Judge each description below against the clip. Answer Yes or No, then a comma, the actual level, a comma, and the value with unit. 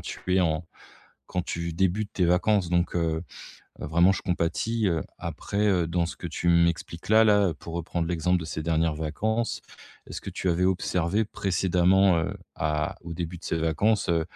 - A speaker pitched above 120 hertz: No, very low, 85 Hz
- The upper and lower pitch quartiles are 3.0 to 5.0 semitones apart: No, narrow, 2.4 semitones